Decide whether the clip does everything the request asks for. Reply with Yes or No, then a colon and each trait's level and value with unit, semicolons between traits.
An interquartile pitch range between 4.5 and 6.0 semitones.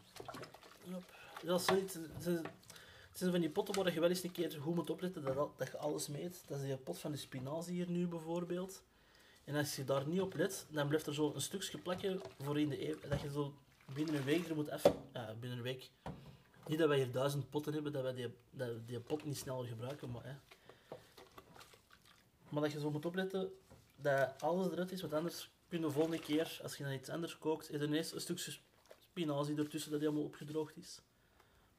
No: average, 3.3 semitones